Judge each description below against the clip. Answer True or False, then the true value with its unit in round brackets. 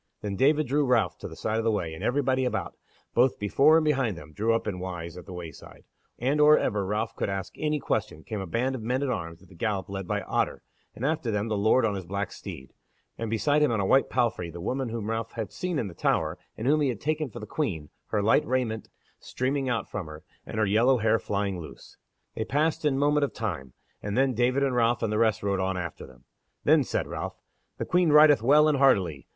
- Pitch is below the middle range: True (115 Hz)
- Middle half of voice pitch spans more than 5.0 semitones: True (5.5 semitones)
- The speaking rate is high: True (245 wpm)